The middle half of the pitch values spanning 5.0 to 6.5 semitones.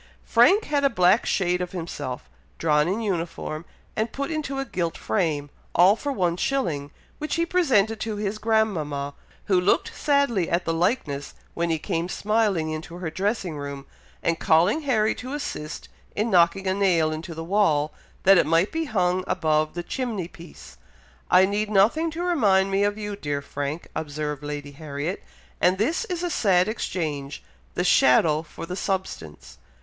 Yes: wide, 5.5 semitones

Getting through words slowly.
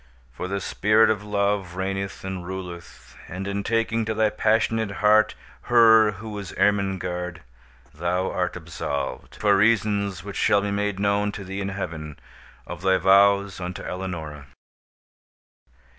No: average, 145 wpm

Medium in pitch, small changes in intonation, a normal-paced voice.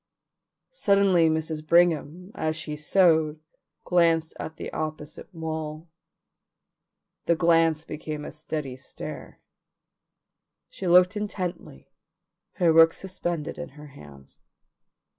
No: medium, 160 Hz; narrow, 2.2 semitones; slow, 105 wpm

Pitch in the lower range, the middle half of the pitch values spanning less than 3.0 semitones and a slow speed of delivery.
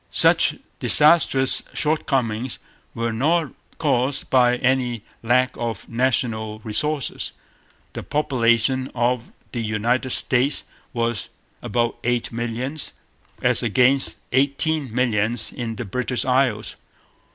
Yes: low, 125 Hz; narrow, 2.4 semitones; slow, 105 wpm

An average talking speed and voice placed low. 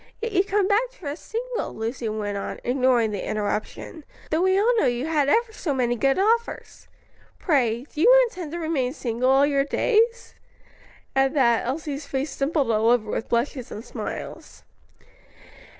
No: average, 170 wpm; very high, 280 Hz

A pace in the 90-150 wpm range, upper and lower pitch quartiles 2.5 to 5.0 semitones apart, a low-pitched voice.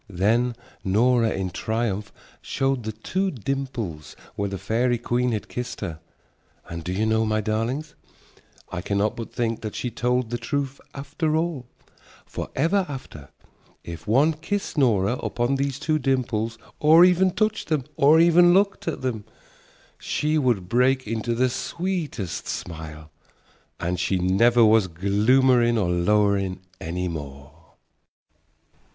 No: average, 140 wpm; wide, 5.5 semitones; low, 120 Hz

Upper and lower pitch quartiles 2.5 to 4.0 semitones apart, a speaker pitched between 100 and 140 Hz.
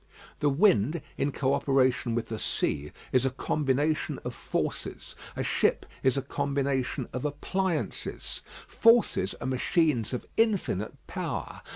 Yes: average, 3.3 semitones; low, 135 Hz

